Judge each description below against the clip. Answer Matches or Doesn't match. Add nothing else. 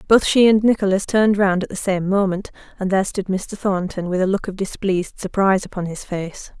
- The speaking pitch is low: Doesn't match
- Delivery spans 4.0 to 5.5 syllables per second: Doesn't match